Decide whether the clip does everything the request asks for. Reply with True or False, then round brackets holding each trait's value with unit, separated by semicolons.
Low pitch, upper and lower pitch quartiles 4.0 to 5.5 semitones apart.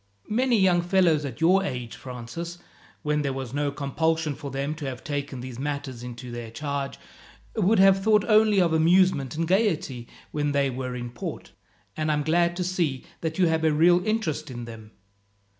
False (150 Hz; 4.8 semitones)